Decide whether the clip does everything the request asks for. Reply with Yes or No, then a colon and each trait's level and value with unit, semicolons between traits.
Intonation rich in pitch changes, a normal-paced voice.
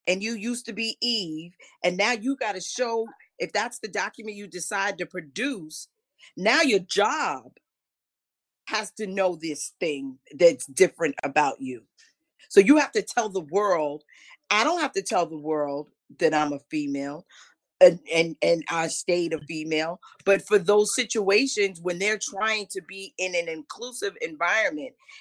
Yes: wide, 6.0 semitones; average, 165 wpm